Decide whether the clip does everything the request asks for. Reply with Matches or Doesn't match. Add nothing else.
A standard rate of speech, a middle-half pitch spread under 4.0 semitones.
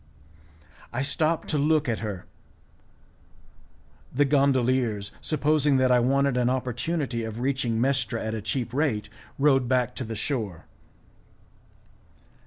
Doesn't match